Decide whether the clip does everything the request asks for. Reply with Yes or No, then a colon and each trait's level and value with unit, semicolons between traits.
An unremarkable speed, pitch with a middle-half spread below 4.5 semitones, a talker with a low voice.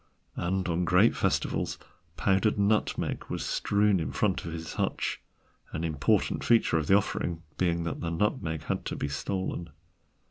Yes: average, 155 wpm; average, 3.5 semitones; very low, 90 Hz